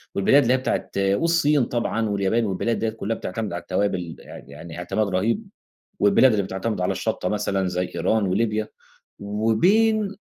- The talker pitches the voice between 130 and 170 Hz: No, low, 105 Hz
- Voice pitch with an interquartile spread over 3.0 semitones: Yes, average, 3.7 semitones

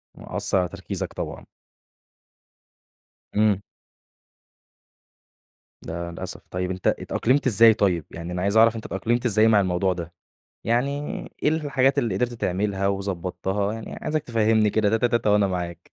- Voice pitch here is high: No, low, 105 Hz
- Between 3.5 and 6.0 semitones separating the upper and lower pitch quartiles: Yes, average, 3.8 semitones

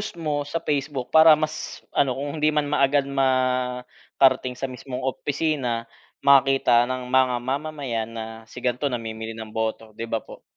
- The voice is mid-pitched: No, low, 130 Hz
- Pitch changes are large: No, average, 2.8 semitones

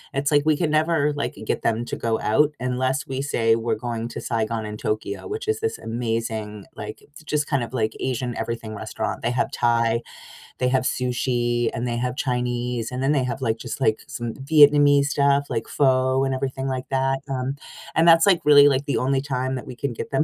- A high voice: No, low, 130 Hz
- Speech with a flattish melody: No, average, 3.2 semitones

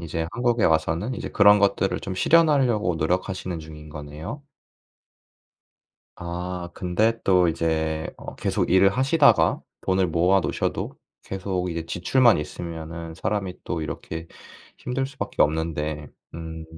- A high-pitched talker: No, very low, 90 Hz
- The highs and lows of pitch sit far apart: No, average, 4.2 semitones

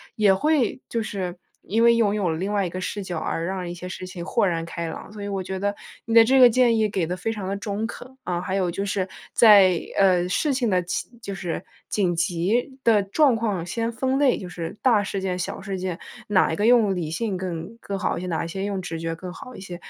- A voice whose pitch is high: Yes, high, 195 Hz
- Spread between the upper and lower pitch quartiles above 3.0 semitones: Yes, average, 3.6 semitones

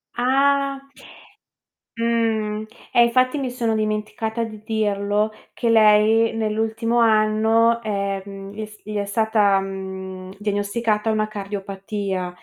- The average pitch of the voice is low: No, high, 215 Hz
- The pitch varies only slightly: Yes, narrow, 2.0 semitones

